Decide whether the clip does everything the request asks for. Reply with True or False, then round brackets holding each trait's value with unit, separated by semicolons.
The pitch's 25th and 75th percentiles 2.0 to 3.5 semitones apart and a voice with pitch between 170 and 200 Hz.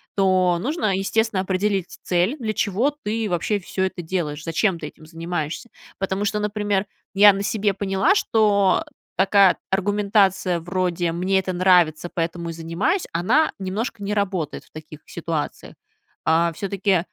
True (3.0 semitones; 190 Hz)